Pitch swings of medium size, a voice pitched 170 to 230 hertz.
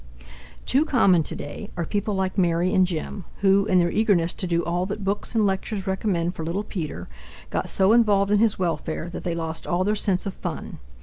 Yes: average, 3.0 semitones; high, 190 Hz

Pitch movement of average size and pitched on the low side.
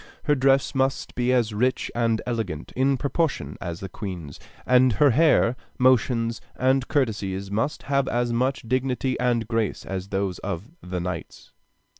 Yes: average, 4.7 semitones; low, 120 Hz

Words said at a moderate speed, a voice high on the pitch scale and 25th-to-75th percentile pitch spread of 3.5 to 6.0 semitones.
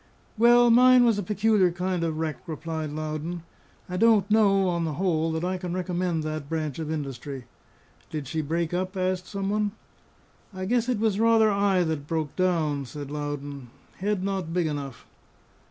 No: average, 175 wpm; medium, 175 Hz; average, 4.3 semitones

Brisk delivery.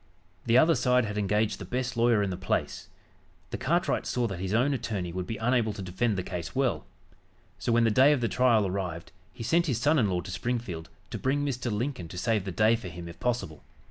Yes: fast, 235 wpm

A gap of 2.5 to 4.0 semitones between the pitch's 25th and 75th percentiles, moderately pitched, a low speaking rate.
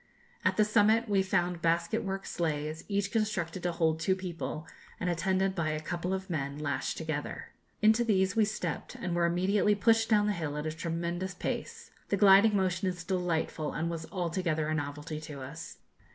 No: average, 3.3 semitones; medium, 175 Hz; average, 185 wpm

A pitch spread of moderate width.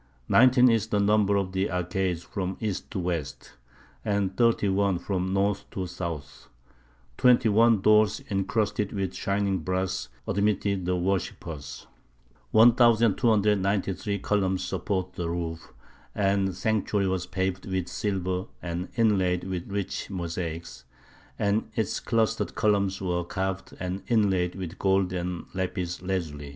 No: narrow, 2.2 semitones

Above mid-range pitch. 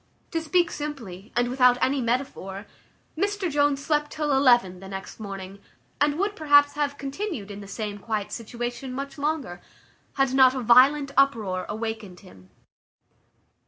Yes: very high, 255 Hz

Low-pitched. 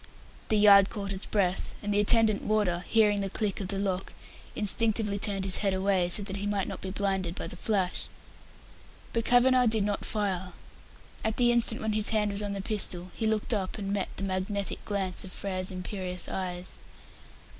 No: high, 200 Hz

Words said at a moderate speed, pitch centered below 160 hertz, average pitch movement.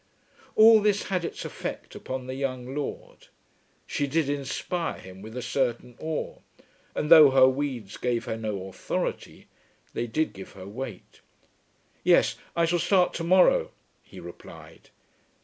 No: average, 150 wpm; low, 135 Hz; wide, 5.9 semitones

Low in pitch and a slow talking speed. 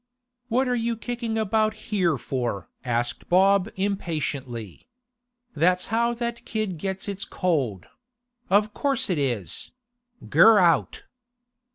No: high, 200 Hz; slow, 105 wpm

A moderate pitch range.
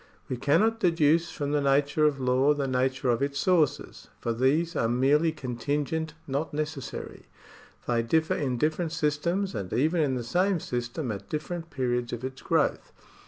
Yes: average, 3.9 semitones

